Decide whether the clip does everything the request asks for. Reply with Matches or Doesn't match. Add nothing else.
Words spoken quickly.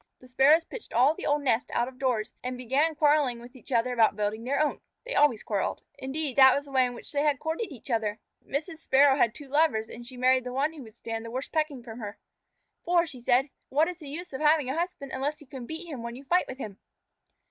Matches